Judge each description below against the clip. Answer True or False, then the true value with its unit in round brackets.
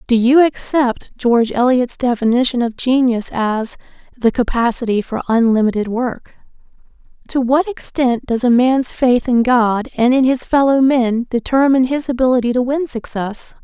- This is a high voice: True (245 Hz)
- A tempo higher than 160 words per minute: False (150 wpm)